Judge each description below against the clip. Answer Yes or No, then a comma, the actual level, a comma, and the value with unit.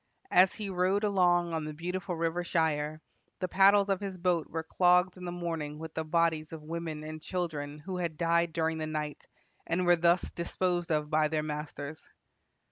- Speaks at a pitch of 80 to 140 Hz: No, medium, 170 Hz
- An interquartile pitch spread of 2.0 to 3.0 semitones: Yes, narrow, 2.5 semitones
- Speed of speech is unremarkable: Yes, average, 190 wpm